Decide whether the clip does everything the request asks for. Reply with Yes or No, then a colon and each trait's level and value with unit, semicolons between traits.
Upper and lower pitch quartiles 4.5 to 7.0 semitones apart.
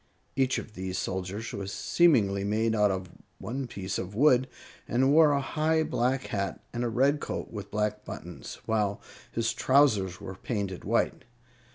Yes: average, 5.2 semitones